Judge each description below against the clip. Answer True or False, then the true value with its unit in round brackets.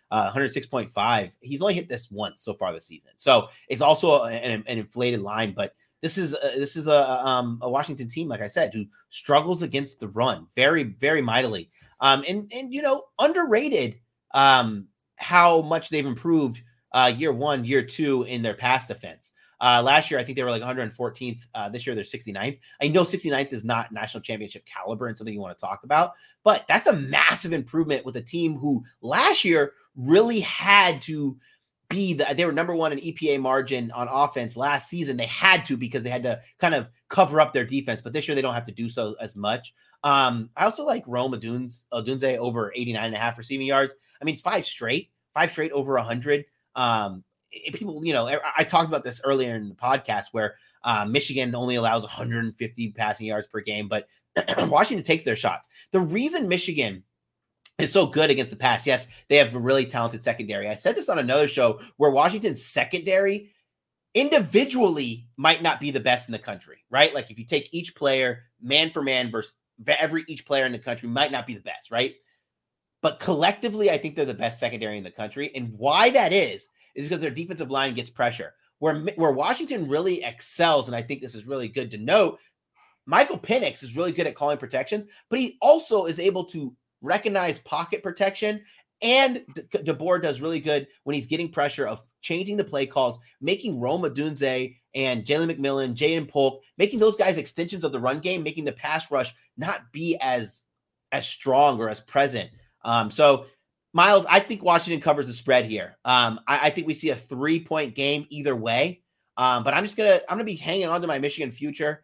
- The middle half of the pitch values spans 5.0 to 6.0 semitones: True (5.3 semitones)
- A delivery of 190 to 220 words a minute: True (205 wpm)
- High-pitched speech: False (140 Hz)